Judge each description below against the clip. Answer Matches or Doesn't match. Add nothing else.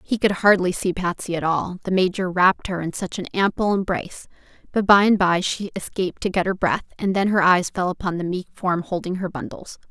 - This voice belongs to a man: Doesn't match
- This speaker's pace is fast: Matches